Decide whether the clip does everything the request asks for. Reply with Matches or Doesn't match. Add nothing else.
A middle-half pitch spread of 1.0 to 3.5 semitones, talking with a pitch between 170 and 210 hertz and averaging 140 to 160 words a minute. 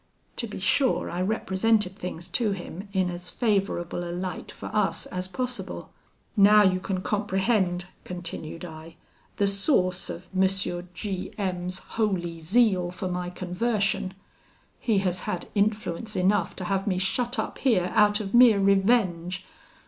Matches